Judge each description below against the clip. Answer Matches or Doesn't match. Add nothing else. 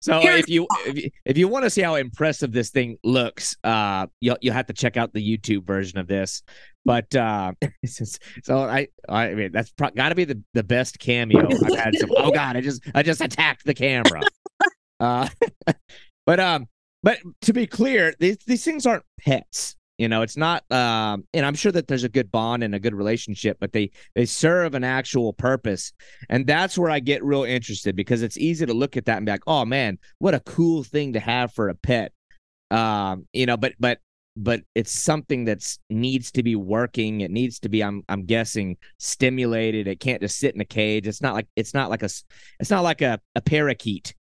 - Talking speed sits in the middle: Doesn't match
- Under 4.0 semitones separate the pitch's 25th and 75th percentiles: Doesn't match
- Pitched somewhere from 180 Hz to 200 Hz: Doesn't match